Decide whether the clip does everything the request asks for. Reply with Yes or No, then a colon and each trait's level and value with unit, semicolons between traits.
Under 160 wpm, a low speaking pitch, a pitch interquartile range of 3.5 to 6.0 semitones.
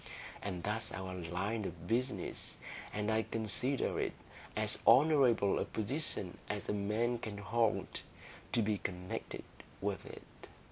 No: slow, 135 wpm; low, 105 Hz; average, 3.1 semitones